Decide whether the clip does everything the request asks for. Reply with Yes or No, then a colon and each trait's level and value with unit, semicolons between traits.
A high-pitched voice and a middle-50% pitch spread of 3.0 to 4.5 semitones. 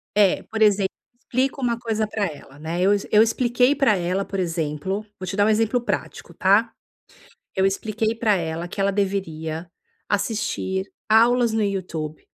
Yes: high, 200 Hz; average, 3.6 semitones